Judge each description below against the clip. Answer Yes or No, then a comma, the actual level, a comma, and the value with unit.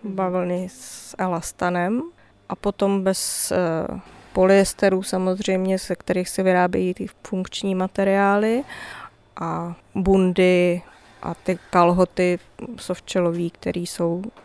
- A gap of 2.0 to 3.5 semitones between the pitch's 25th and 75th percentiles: No, narrow, 1.6 semitones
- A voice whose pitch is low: No, medium, 185 Hz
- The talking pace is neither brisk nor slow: No, slow, 95 wpm